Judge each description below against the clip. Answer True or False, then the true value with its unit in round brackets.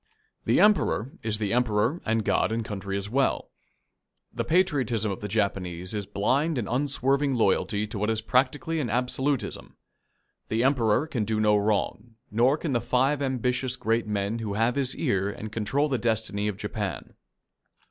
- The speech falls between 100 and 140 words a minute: False (170 wpm)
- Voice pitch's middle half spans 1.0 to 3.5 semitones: False (4.0 semitones)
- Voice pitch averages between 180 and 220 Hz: False (115 Hz)